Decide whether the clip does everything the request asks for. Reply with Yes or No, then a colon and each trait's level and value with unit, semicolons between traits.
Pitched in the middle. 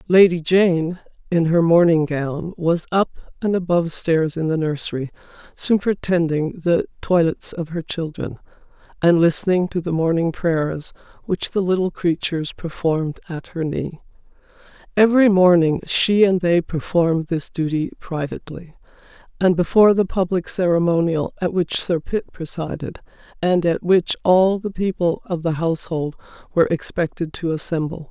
Yes: medium, 170 Hz